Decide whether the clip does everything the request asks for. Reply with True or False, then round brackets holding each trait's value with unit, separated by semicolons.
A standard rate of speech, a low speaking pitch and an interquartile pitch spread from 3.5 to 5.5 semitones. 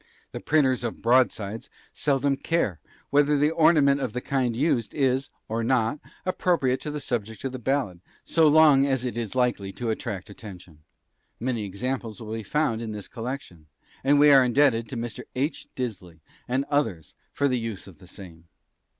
True (175 wpm; 125 Hz; 4.2 semitones)